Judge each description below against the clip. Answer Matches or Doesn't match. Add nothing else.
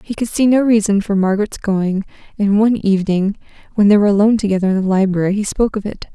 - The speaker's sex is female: Matches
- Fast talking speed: Matches